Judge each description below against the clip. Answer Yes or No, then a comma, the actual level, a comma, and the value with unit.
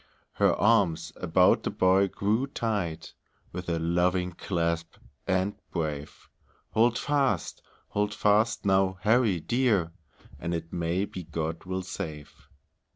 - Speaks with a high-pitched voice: No, very low, 95 Hz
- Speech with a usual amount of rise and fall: Yes, average, 3.8 semitones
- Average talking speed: No, slow, 125 wpm